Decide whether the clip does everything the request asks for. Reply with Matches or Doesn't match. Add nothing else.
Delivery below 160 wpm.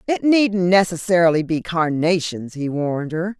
Matches